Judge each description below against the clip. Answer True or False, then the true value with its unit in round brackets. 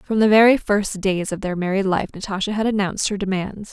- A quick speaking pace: True (225 wpm)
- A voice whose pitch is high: True (200 Hz)